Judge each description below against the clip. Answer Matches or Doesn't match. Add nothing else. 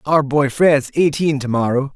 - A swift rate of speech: Matches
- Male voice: Matches